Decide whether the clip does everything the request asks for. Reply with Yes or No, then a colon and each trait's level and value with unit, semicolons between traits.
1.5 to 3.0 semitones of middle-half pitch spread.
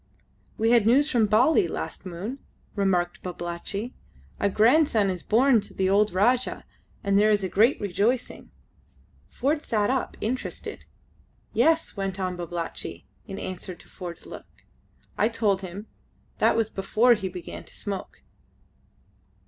No: average, 4.0 semitones